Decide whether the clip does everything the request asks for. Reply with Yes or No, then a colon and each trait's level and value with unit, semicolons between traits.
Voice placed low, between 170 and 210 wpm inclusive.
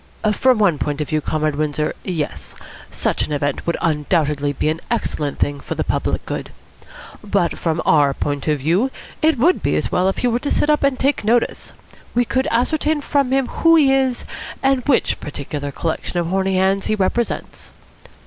No: high, 190 Hz; average, 190 wpm